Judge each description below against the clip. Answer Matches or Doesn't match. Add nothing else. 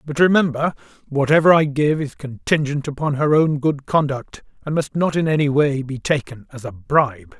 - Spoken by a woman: Doesn't match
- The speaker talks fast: Doesn't match